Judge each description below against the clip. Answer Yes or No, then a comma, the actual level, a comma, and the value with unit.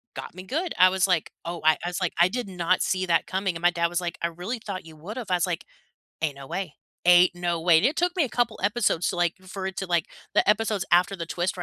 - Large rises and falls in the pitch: No, narrow, 2.4 semitones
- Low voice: No, medium, 180 Hz